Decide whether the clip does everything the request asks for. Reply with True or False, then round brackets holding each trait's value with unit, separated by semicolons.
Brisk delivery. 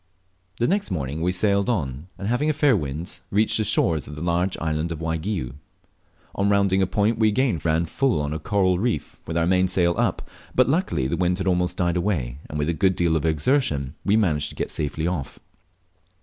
True (210 wpm)